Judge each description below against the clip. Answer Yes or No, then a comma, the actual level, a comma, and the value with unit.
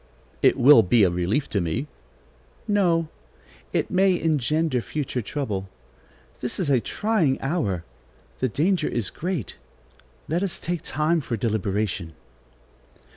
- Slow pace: Yes, slow, 130 wpm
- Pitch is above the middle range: No, low, 135 Hz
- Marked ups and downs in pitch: Yes, wide, 7.5 semitones